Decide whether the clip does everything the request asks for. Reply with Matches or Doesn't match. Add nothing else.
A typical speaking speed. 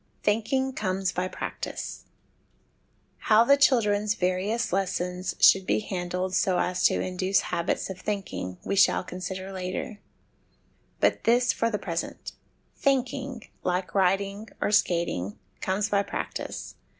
Doesn't match